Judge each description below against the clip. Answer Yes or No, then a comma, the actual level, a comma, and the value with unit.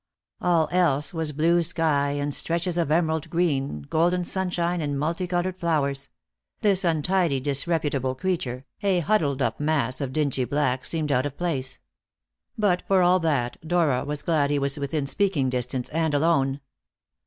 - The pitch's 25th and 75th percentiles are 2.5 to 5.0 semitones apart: Yes, average, 3.9 semitones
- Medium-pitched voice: Yes, medium, 155 Hz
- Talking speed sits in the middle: Yes, average, 155 wpm